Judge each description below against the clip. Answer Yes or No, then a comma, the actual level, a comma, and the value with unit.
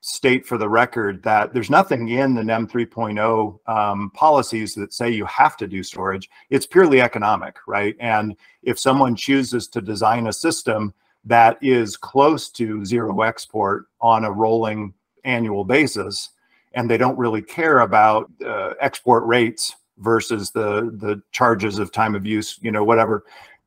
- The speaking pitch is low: Yes, low, 115 Hz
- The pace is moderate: Yes, average, 160 wpm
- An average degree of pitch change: No, narrow, 2.1 semitones